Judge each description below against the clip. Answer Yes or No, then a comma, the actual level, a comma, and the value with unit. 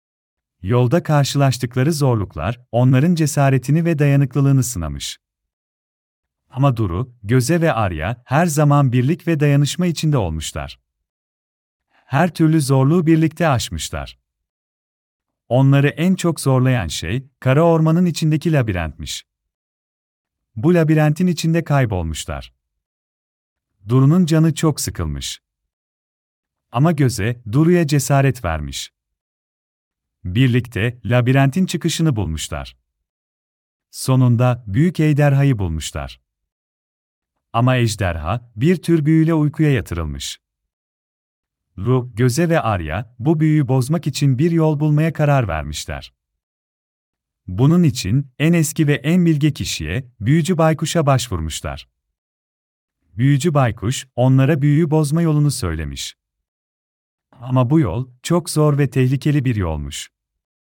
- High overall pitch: No, low, 125 Hz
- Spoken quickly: No, average, 100 wpm